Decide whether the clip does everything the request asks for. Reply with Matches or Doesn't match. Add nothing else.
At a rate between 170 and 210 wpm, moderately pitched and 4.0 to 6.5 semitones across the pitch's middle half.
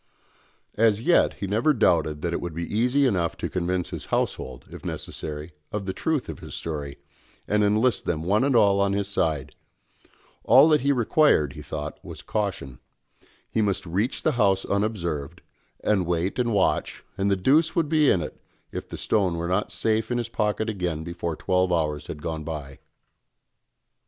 Doesn't match